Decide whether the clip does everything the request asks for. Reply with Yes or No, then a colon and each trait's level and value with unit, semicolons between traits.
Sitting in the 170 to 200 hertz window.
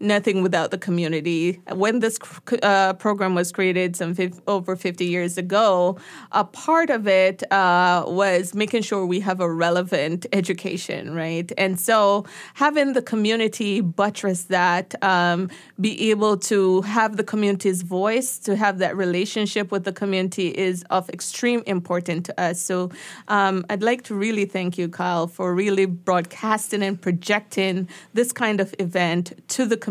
Yes: high, 190 Hz